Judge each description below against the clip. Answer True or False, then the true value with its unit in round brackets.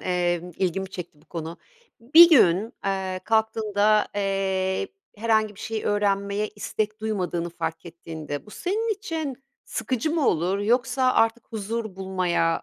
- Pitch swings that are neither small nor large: True (3.8 semitones)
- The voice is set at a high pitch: True (205 Hz)